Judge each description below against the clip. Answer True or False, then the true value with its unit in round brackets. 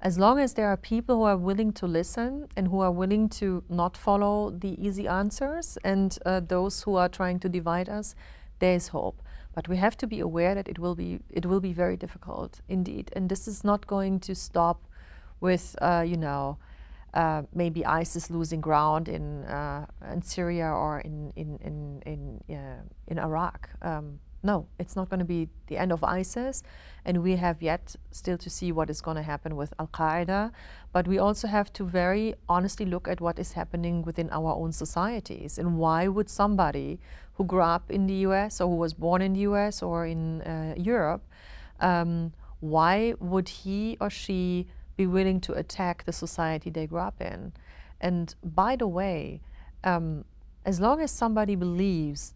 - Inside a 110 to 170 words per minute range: False (190 wpm)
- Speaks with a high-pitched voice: False (180 Hz)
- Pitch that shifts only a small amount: False (3.0 semitones)